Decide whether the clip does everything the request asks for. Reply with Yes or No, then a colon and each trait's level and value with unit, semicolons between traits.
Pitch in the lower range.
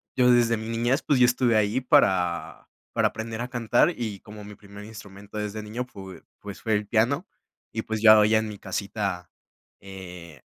Yes: low, 110 Hz